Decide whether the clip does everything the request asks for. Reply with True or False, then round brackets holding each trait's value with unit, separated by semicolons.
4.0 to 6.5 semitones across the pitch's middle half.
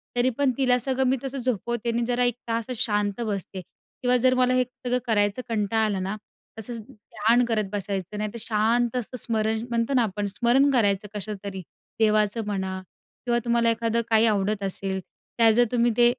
False (2.8 semitones)